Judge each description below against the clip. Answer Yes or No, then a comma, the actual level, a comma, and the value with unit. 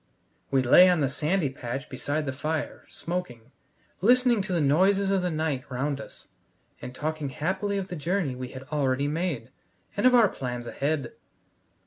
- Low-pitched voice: No, medium, 150 Hz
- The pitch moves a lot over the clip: Yes, wide, 5.7 semitones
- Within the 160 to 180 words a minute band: Yes, average, 170 wpm